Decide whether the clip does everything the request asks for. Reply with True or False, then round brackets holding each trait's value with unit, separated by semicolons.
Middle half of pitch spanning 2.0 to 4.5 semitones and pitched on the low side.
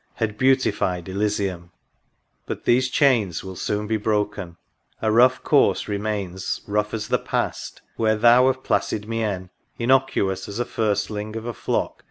True (2.9 semitones; 105 Hz)